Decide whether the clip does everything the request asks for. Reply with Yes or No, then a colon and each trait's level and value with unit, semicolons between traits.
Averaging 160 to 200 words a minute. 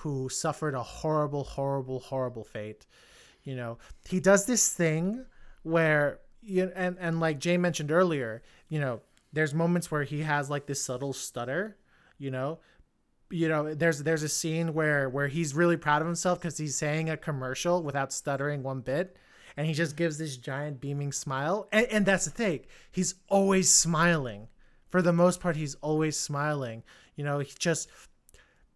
Yes: average, 175 wpm